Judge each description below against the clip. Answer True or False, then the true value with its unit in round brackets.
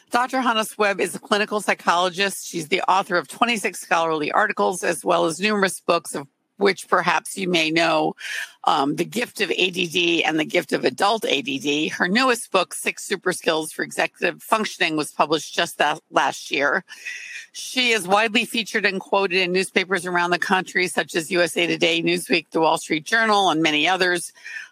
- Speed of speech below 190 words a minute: True (180 wpm)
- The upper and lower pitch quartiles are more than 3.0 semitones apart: True (3.8 semitones)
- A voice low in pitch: False (185 Hz)